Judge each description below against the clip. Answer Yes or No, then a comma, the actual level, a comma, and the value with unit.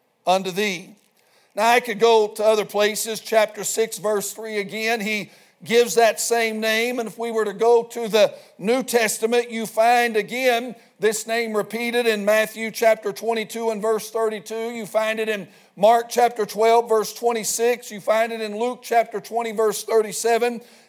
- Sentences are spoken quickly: No, average, 170 wpm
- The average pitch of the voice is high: Yes, high, 225 Hz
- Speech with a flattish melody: Yes, narrow, 1.5 semitones